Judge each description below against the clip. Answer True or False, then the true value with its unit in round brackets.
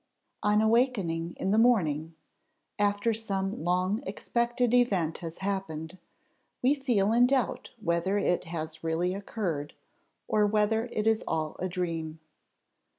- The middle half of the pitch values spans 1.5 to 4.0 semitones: False (5.0 semitones)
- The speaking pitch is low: False (195 Hz)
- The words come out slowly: True (130 wpm)